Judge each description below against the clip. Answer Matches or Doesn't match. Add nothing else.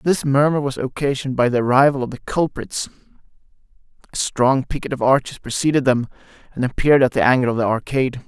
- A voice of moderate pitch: Doesn't match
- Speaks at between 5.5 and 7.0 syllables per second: Matches